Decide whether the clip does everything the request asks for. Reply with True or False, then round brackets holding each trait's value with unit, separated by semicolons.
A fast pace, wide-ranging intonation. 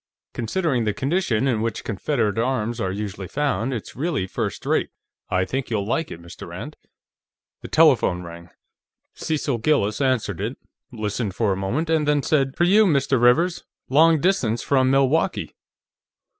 False (155 wpm; 5.8 semitones)